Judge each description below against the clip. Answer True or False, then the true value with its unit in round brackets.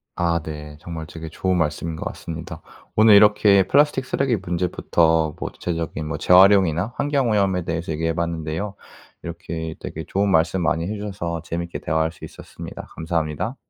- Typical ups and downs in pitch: True (3.5 semitones)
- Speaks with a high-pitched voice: False (85 Hz)